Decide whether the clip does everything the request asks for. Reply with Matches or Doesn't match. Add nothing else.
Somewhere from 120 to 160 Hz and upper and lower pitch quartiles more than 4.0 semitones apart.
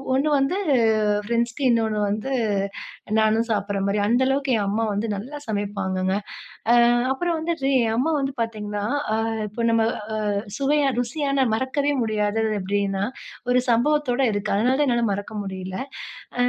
Doesn't match